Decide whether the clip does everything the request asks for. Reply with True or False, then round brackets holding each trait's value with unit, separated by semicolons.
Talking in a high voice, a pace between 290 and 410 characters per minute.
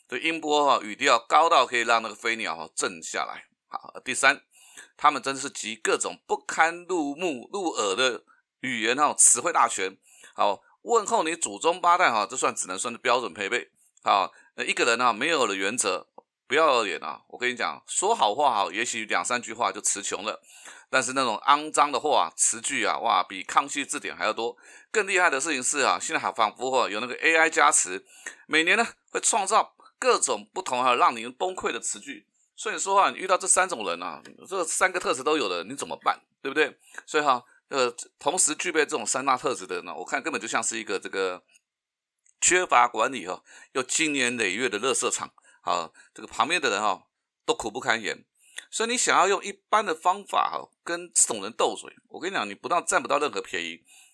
False (175 Hz; 300 characters per minute)